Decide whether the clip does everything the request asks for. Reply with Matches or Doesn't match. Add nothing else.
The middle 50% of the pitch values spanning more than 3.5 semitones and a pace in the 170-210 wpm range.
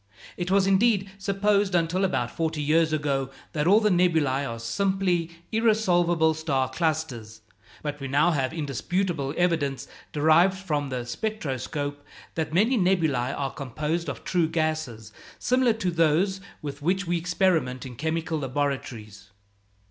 Doesn't match